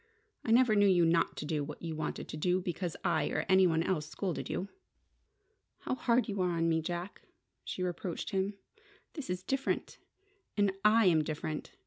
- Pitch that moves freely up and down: No, average, 3.6 semitones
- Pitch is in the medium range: Yes, medium, 180 Hz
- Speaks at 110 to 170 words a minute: No, average, 185 wpm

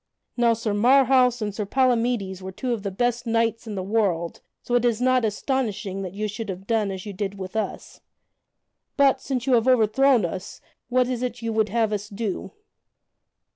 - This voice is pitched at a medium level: No, high, 225 Hz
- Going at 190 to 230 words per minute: Yes, average, 195 wpm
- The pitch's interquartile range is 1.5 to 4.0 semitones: Yes, average, 3.5 semitones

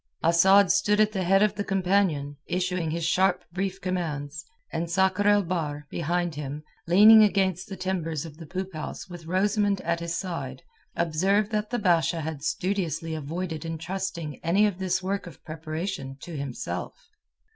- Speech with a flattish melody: No, average, 3.3 semitones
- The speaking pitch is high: No, medium, 175 Hz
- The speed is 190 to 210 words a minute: No, average, 165 wpm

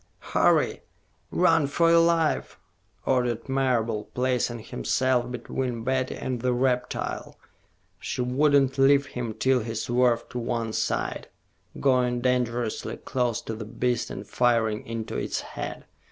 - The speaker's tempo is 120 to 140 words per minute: Yes, slow, 135 wpm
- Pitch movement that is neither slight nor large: No, narrow, 2.1 semitones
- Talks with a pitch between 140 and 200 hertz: No, low, 125 Hz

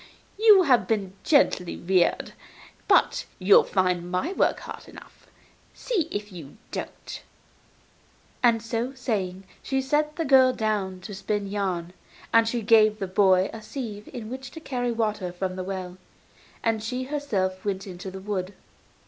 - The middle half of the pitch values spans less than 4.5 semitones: No, average, 5.0 semitones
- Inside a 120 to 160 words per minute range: Yes, average, 155 wpm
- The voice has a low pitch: No, high, 210 Hz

